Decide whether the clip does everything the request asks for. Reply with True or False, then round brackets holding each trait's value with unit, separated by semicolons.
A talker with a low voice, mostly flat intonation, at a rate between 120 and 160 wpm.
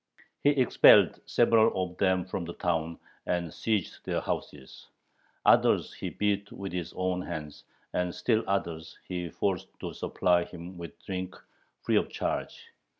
True (90 Hz; 2.3 semitones; 150 wpm)